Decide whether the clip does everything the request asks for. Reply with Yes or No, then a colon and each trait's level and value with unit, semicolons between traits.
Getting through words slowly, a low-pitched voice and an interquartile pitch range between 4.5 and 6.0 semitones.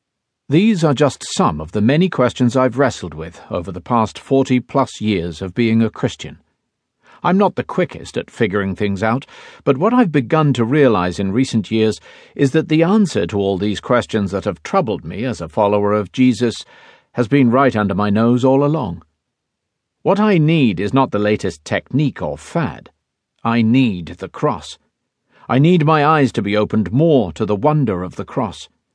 No: average, 190 wpm; low, 115 Hz; wide, 5.4 semitones